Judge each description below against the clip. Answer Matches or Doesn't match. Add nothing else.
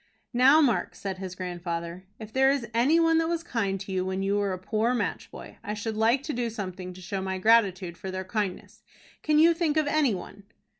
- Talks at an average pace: Doesn't match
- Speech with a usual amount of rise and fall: Doesn't match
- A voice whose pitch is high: Matches